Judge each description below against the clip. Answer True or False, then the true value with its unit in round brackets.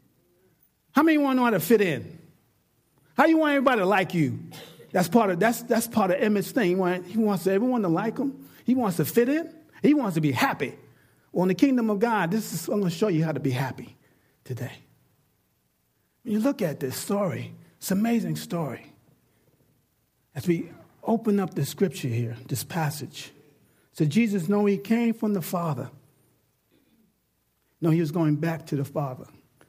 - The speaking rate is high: False (185 wpm)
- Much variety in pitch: True (7.5 semitones)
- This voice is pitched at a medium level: True (175 Hz)